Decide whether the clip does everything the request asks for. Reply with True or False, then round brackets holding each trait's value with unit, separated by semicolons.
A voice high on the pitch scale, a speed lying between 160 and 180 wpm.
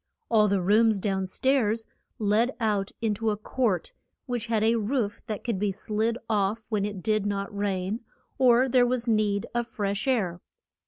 True (215 Hz; 175 wpm)